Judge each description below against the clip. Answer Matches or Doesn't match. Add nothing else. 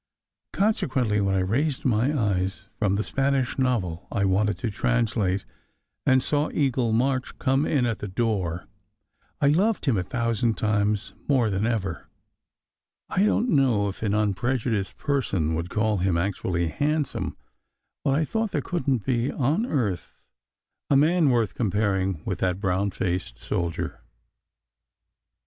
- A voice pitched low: Matches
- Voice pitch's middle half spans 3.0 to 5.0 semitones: Doesn't match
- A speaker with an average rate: Matches